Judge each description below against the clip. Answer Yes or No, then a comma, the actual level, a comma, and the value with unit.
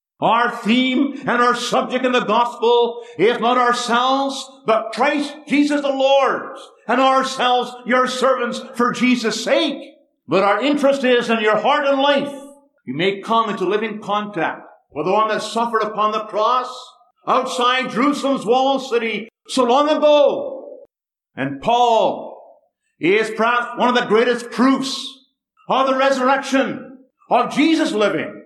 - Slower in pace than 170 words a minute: Yes, average, 145 wpm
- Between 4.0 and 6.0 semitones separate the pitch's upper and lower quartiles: No, average, 2.7 semitones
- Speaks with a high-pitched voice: Yes, very high, 250 Hz